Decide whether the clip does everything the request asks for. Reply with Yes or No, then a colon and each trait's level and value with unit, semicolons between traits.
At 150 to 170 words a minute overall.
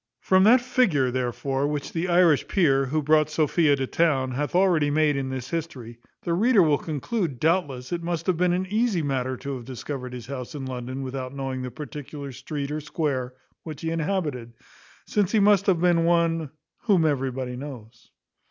No: average, 185 wpm